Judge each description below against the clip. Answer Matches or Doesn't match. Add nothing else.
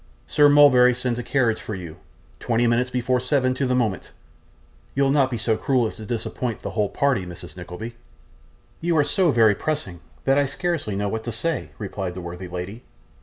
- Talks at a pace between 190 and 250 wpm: Matches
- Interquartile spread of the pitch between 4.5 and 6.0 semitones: Matches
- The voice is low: Matches